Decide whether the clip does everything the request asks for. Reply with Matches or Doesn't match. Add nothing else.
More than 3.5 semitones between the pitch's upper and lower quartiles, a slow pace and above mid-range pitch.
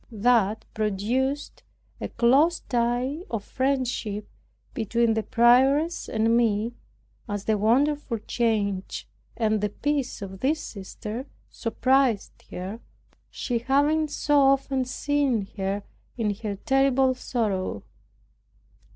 Matches